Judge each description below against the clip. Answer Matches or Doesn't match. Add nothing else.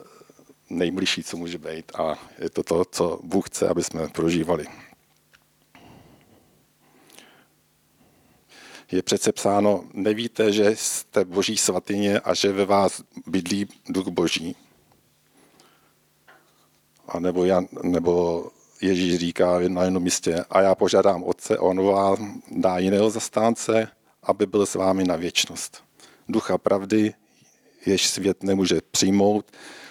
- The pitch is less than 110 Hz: Matches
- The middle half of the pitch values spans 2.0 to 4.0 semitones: Matches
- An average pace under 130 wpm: Matches